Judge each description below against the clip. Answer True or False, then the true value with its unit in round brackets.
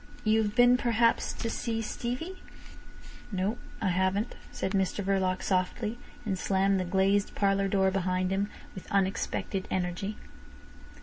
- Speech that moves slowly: True (130 wpm)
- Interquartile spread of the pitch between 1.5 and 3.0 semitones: True (2.5 semitones)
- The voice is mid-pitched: False (195 Hz)